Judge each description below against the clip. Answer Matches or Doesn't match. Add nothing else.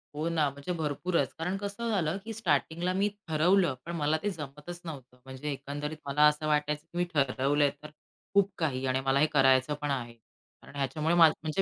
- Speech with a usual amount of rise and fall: Matches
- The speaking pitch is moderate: Matches